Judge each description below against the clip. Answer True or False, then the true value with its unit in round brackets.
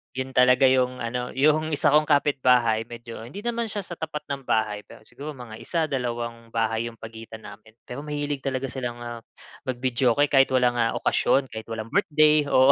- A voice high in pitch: False (125 Hz)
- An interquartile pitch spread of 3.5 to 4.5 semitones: True (3.8 semitones)